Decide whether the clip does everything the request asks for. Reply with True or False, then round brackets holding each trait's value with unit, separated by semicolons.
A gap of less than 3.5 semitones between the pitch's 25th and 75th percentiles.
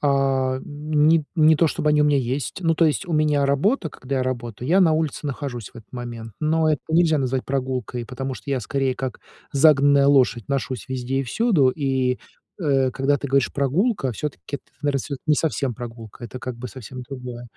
True (2.9 semitones)